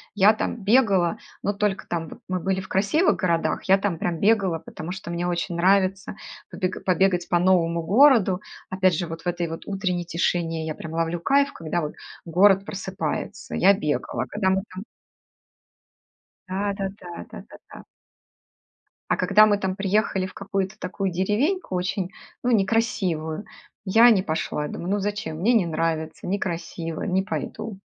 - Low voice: No, medium, 185 Hz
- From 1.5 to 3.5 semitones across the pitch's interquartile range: Yes, average, 2.8 semitones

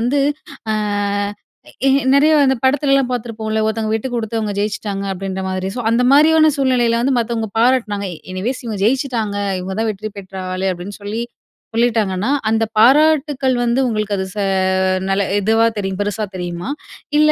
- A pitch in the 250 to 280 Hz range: No, high, 225 Hz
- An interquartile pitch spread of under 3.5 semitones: No, average, 4.2 semitones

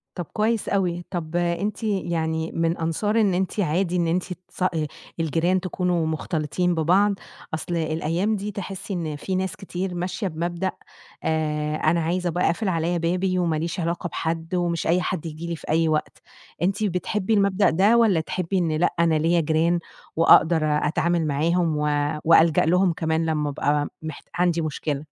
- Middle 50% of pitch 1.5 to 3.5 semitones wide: Yes, narrow, 2.5 semitones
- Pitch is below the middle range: No, medium, 170 Hz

